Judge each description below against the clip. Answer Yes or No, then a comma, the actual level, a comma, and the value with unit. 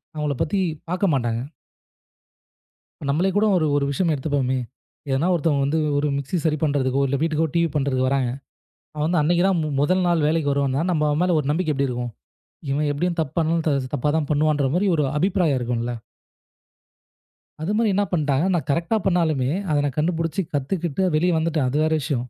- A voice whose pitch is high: No, medium, 150 Hz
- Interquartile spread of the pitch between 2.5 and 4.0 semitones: Yes, average, 3.3 semitones